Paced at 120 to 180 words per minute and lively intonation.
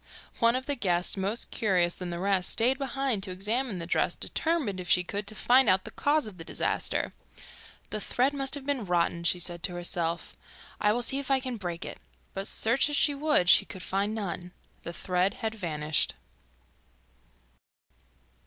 No: average, 190 wpm; wide, 6.4 semitones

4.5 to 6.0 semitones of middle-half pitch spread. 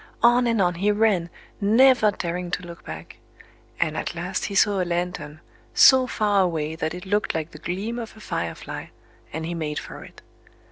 No: average, 4.1 semitones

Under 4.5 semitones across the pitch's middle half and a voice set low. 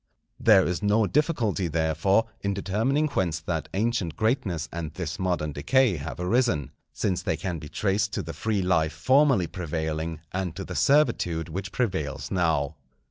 No: average, 5.2 semitones; very low, 90 Hz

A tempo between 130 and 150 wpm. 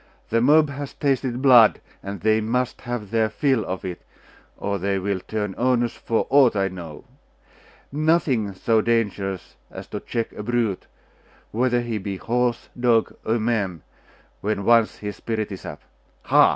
No: average, 160 wpm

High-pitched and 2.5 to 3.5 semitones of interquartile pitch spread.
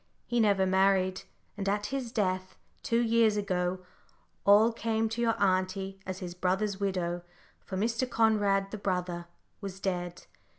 Yes: high, 195 Hz; average, 2.9 semitones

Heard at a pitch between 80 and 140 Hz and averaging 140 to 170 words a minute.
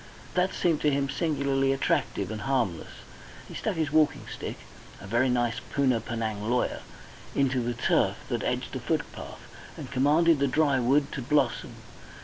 Yes: low, 135 Hz; average, 160 wpm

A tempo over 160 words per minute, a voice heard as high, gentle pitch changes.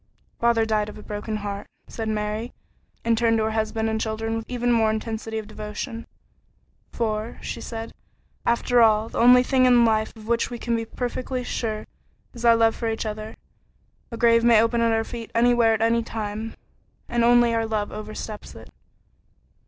Yes: average, 185 wpm; high, 225 Hz; narrow, 1.3 semitones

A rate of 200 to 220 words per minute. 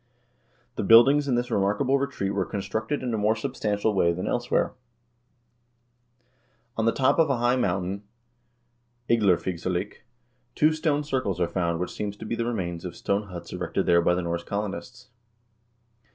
No: average, 160 wpm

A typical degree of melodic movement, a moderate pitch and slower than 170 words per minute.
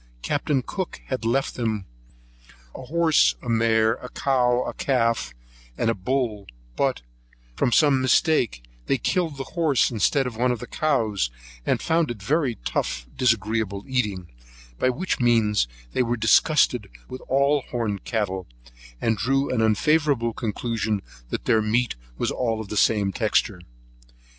No: average, 3.7 semitones; low, 120 Hz; average, 155 wpm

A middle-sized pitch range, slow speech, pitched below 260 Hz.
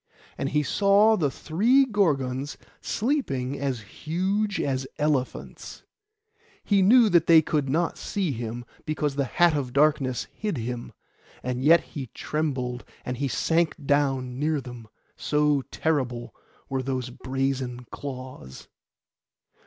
Yes: average, 4.4 semitones; slow, 130 wpm; medium, 140 Hz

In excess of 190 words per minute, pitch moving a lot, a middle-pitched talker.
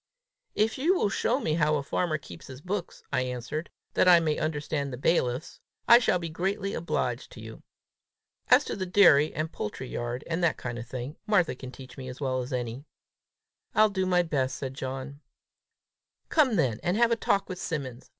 Yes: average, 200 wpm; wide, 6.0 semitones; medium, 155 Hz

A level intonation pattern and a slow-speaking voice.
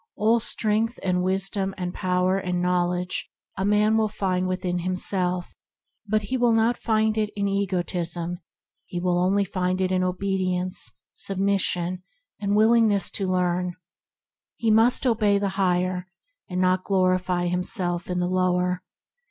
No: narrow, 2.2 semitones; average, 145 wpm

